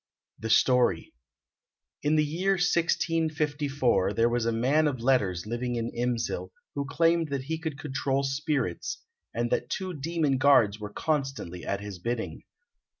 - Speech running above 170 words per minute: No, average, 150 wpm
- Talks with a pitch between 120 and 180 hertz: Yes, low, 135 Hz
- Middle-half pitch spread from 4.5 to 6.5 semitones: Yes, average, 4.8 semitones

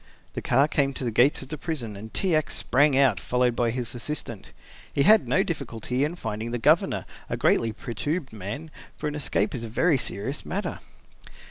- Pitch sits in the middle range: No, low, 130 Hz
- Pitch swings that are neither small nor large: Yes, average, 4.6 semitones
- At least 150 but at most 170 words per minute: No, average, 200 wpm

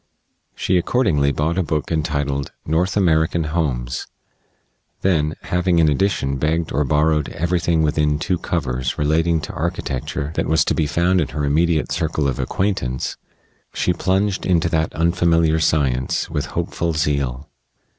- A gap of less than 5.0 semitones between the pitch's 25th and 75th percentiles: Yes, average, 2.9 semitones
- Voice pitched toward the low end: Yes, very low, 80 Hz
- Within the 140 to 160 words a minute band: Yes, average, 145 wpm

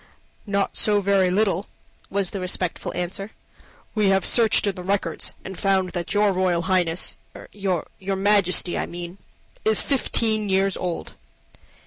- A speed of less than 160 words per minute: Yes, average, 140 wpm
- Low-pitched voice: No, high, 195 Hz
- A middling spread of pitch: No, narrow, 1.9 semitones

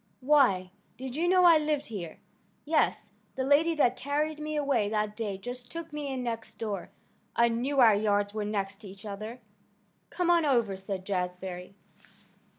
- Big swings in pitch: Yes, wide, 6.4 semitones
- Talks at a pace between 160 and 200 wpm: Yes, average, 170 wpm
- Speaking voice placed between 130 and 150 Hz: No, high, 235 Hz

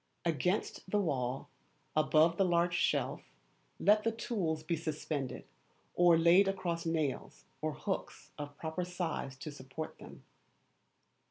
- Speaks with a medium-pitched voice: Yes, medium, 165 Hz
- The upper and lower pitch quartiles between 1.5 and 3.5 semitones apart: Yes, average, 2.8 semitones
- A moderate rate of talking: No, slow, 125 wpm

